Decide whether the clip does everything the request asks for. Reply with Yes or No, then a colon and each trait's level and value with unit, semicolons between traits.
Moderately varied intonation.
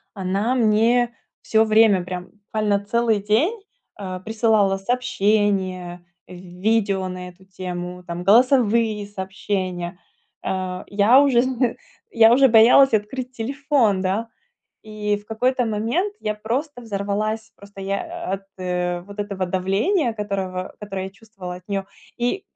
Yes: average, 3.5 semitones